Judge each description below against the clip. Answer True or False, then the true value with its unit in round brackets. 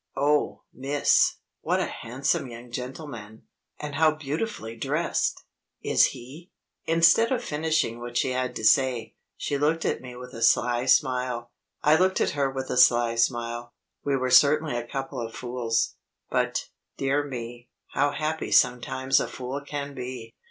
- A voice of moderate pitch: False (130 Hz)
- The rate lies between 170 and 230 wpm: False (160 wpm)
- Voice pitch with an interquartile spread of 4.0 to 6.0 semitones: False (3.4 semitones)